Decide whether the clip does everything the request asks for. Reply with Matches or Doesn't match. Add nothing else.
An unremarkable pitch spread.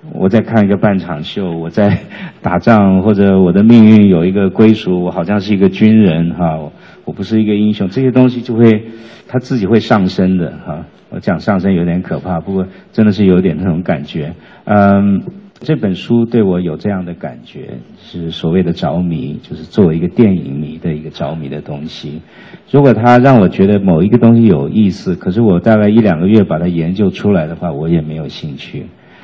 Matches